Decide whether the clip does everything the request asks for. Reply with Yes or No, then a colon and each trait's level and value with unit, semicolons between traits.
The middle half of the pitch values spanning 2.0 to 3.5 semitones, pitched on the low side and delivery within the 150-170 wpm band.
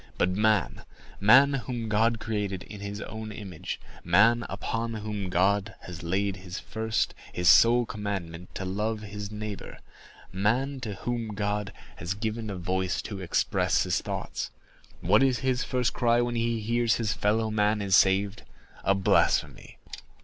No: average, 2.8 semitones; low, 105 Hz; average, 140 wpm